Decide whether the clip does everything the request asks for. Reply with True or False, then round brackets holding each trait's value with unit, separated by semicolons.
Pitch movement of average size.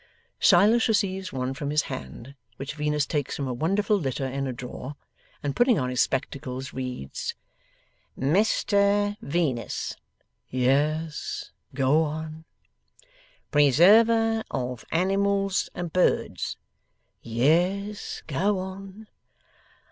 False (6.7 semitones)